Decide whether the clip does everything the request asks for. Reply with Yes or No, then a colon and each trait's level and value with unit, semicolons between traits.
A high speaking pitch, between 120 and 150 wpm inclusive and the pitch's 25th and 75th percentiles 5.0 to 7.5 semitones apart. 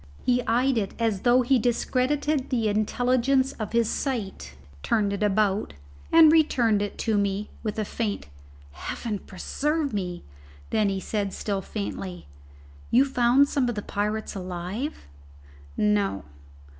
No: high, 220 Hz; average, 140 wpm; average, 4.1 semitones